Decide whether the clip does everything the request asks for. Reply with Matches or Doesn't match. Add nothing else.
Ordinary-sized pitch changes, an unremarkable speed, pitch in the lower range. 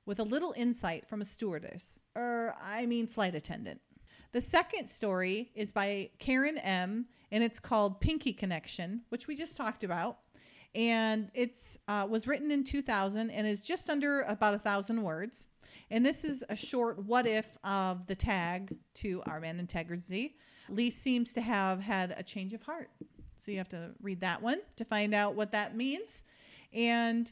Doesn't match